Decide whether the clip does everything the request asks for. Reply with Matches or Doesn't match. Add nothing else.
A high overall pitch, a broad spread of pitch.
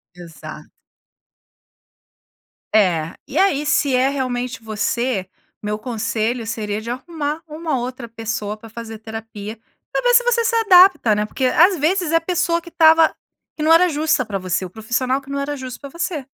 Matches